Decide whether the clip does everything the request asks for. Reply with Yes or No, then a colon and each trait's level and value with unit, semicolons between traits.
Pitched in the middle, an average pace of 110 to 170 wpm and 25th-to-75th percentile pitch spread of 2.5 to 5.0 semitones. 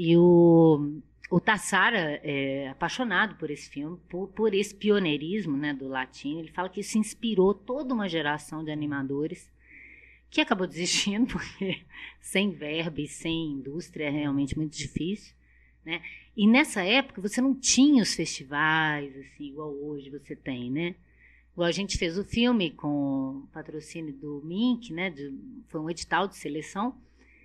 No: medium, 165 Hz; average, 155 wpm; wide, 5.4 semitones